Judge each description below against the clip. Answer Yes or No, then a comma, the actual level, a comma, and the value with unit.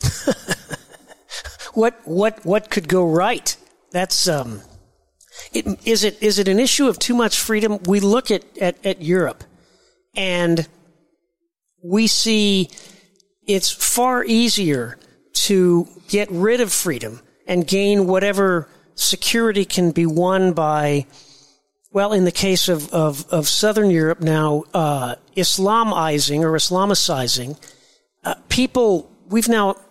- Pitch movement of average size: Yes, average, 4.2 semitones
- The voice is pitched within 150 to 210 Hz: Yes, medium, 185 Hz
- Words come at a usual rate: No, slow, 125 wpm